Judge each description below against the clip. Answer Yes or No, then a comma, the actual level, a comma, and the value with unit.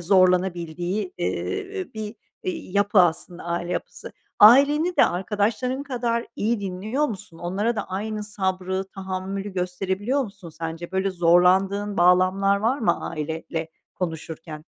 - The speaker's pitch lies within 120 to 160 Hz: No, high, 190 Hz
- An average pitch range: Yes, average, 3.1 semitones